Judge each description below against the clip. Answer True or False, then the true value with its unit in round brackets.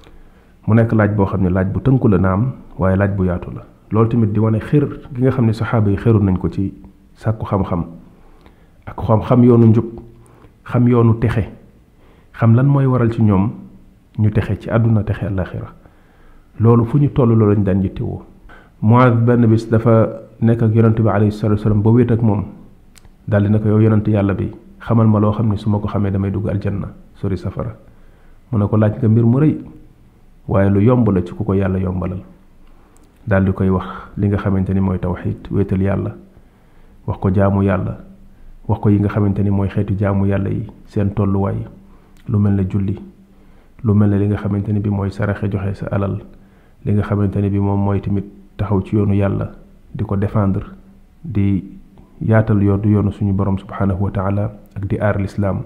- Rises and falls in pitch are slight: True (2.2 semitones)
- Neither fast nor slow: False (75 wpm)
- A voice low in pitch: True (100 Hz)